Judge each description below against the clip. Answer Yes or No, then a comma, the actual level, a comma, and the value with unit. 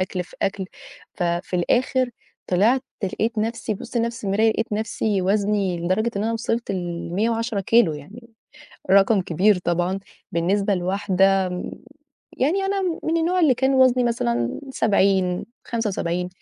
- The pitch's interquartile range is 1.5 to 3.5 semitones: No, average, 4.3 semitones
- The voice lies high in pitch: Yes, high, 205 Hz